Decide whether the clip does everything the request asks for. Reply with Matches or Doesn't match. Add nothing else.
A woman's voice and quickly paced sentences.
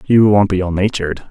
Doesn't match